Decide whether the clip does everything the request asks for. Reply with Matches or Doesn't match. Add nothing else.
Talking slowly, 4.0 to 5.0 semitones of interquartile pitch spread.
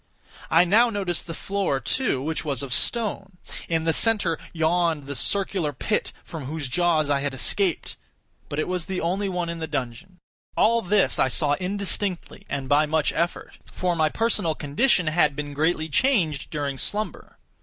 Doesn't match